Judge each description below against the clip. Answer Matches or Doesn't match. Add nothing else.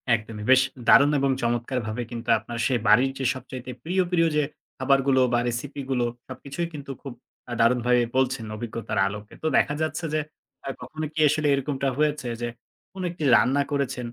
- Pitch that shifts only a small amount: Doesn't match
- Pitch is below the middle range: Matches